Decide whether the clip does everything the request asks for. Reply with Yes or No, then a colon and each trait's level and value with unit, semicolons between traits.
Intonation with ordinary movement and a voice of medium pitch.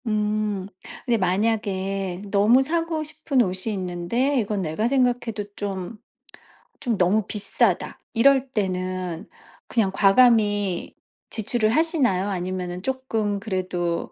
No: average, 4.4 semitones; high, 210 Hz